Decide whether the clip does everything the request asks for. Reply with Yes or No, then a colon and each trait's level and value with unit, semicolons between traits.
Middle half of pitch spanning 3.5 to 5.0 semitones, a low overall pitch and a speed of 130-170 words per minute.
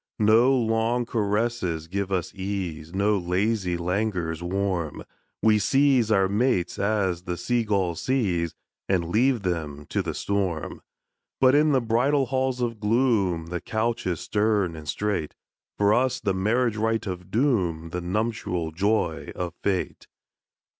Yes: average, 4.6 semitones; low, 100 Hz; average, 145 wpm